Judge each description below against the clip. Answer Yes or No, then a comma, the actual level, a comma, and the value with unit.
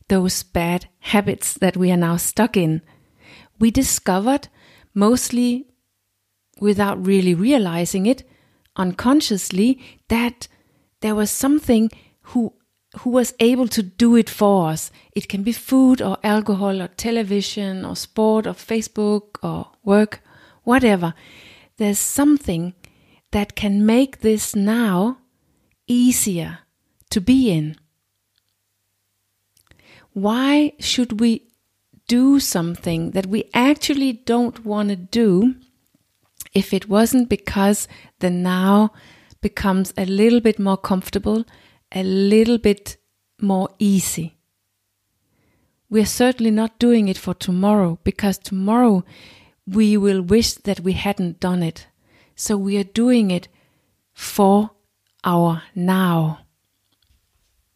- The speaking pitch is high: Yes, high, 200 Hz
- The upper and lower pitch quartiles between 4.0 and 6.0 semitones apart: Yes, average, 4.3 semitones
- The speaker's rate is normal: No, slow, 115 wpm